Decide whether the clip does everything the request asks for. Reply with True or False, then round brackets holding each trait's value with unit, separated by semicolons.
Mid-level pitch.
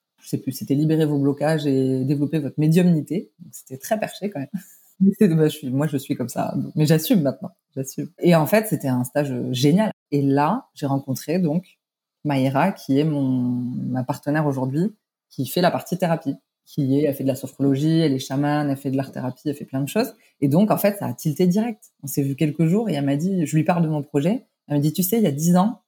True (150 Hz)